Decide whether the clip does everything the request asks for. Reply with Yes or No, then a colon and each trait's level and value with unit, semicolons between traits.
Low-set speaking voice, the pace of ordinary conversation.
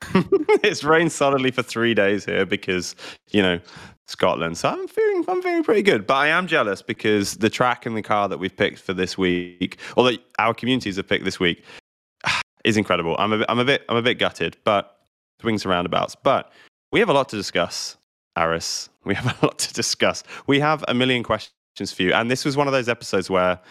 No: low, 110 Hz; fast, 220 wpm